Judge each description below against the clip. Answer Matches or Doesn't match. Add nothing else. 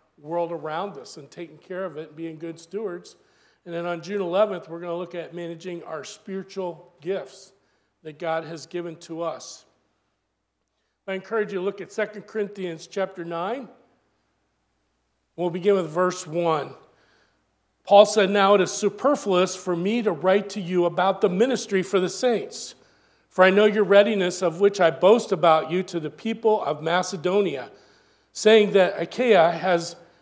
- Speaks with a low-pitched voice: Doesn't match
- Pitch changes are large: Doesn't match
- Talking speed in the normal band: Matches